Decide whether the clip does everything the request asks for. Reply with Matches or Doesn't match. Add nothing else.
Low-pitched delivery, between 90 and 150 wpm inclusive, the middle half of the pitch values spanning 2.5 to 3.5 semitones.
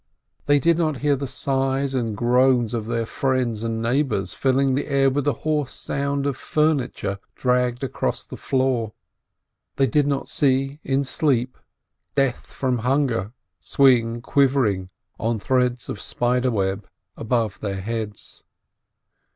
Matches